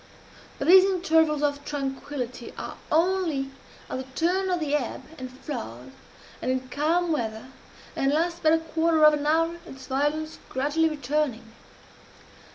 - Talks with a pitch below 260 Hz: No, very high, 295 Hz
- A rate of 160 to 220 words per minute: No, average, 150 wpm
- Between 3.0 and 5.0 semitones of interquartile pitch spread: Yes, average, 3.5 semitones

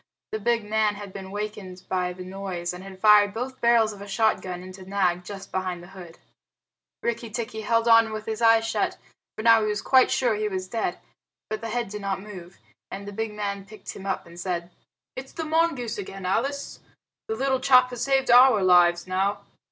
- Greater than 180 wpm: Yes, fast, 205 wpm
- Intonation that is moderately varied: Yes, average, 3.3 semitones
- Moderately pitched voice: No, high, 210 Hz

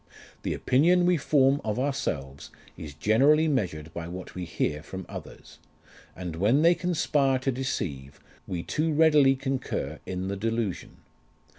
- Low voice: Yes, low, 120 Hz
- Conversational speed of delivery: Yes, average, 145 wpm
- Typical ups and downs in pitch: No, wide, 8.7 semitones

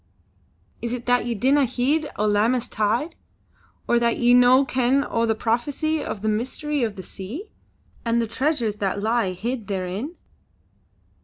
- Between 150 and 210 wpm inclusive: Yes, average, 160 wpm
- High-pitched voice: Yes, high, 235 Hz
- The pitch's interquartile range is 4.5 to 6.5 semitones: No, average, 3.4 semitones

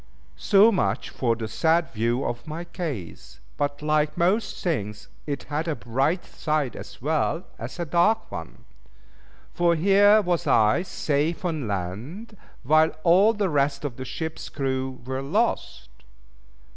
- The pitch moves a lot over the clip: No, average, 5.0 semitones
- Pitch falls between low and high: Yes, medium, 150 Hz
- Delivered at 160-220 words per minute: No, average, 145 wpm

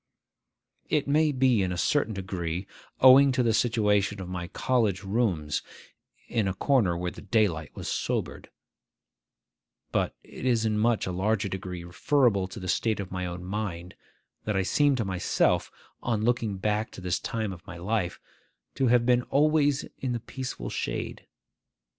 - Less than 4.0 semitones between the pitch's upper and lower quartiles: No, average, 4.9 semitones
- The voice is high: No, low, 105 Hz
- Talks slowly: No, average, 165 wpm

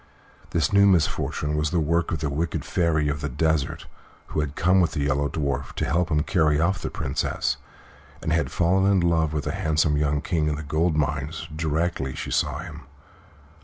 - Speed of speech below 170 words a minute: No, average, 200 wpm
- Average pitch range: No, narrow, 2.3 semitones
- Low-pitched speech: Yes, very low, 80 Hz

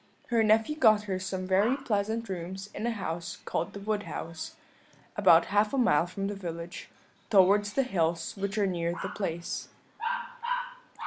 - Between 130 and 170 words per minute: Yes, average, 165 wpm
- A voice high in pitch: Yes, high, 195 Hz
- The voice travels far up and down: No, average, 3.7 semitones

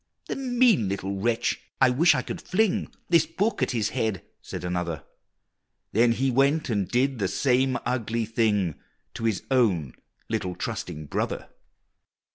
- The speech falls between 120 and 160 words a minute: Yes, average, 150 wpm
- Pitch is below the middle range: Yes, low, 115 Hz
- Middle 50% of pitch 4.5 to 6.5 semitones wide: Yes, wide, 5.6 semitones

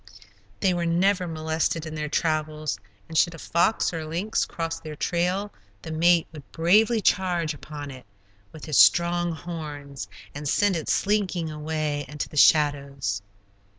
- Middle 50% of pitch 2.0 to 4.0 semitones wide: Yes, narrow, 2.5 semitones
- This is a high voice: No, medium, 160 Hz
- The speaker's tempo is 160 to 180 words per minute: No, average, 150 wpm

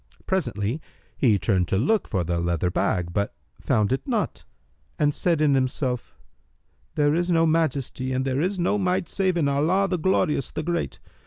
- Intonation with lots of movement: Yes, wide, 7.3 semitones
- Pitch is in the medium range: Yes, medium, 145 Hz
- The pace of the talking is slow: No, average, 175 wpm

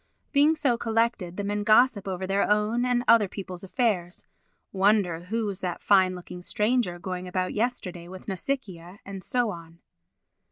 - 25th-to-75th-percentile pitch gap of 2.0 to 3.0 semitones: No, average, 4.1 semitones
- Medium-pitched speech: No, high, 200 Hz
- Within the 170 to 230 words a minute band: No, average, 155 wpm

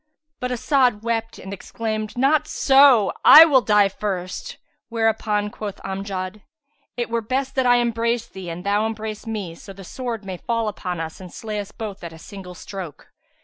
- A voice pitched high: Yes, high, 215 Hz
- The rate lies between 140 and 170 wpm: No, average, 180 wpm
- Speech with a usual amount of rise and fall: Yes, average, 3.3 semitones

